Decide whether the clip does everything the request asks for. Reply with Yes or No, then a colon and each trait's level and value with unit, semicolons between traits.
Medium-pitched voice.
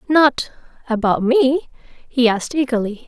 No: very high, 255 Hz